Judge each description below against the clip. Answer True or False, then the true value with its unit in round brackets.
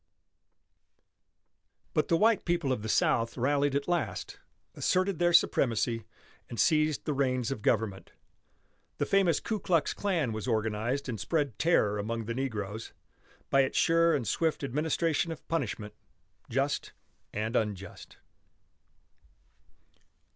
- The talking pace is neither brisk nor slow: False (125 wpm)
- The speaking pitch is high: False (135 Hz)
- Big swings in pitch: True (6.5 semitones)